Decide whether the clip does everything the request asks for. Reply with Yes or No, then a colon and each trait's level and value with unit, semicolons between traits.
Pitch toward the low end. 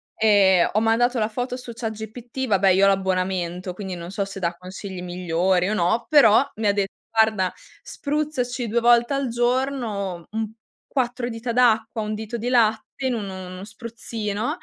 No: high, 220 Hz